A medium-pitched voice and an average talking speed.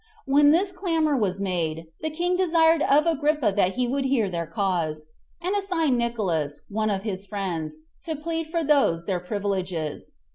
No: high, 235 Hz; average, 170 wpm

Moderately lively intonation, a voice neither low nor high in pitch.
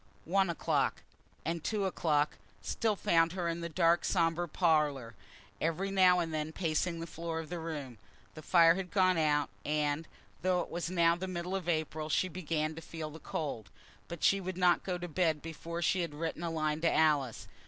No: narrow, 2.3 semitones; medium, 165 Hz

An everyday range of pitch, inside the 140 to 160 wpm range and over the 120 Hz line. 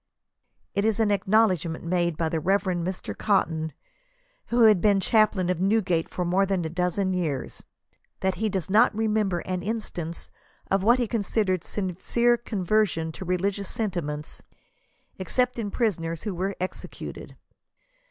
Yes: average, 3.6 semitones; average, 150 wpm; high, 190 Hz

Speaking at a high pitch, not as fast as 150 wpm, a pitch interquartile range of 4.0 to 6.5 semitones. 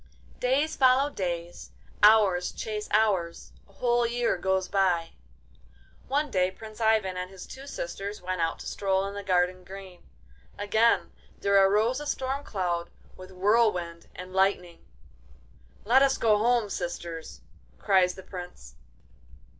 No: high, 195 Hz; average, 140 wpm; average, 3.6 semitones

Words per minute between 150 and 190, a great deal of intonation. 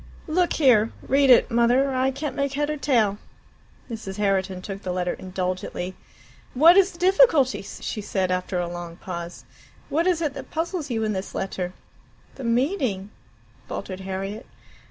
Yes: average, 165 wpm; wide, 6.8 semitones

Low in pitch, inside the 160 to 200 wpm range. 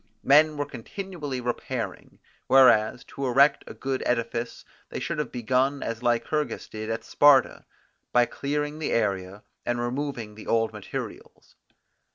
No: low, 125 Hz; average, 140 wpm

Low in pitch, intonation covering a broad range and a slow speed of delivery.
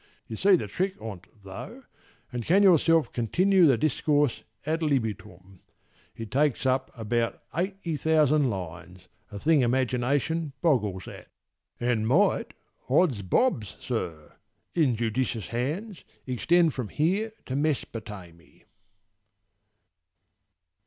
Yes: low, 130 Hz; wide, 6.7 semitones; slow, 110 wpm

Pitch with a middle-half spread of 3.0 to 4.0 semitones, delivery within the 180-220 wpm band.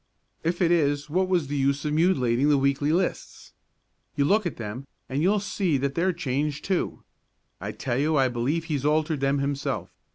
Yes: average, 3.6 semitones; average, 190 wpm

